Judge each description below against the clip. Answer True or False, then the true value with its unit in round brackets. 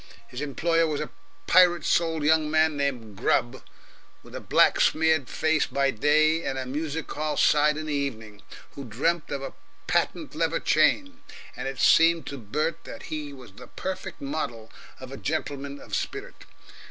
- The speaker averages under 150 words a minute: False (170 wpm)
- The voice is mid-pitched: True (150 Hz)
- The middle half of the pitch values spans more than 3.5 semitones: False (3.1 semitones)